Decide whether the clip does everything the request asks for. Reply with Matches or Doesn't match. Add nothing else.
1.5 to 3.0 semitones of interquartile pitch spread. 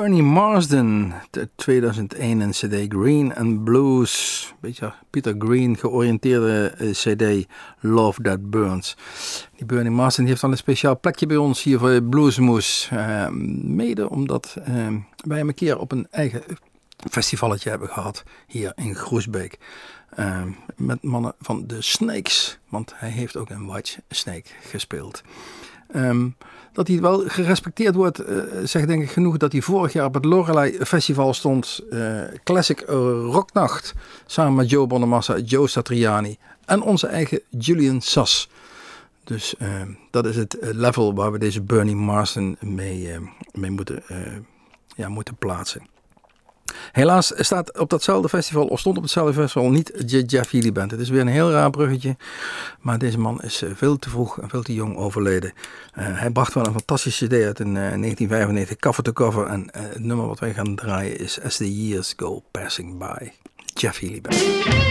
Doesn't match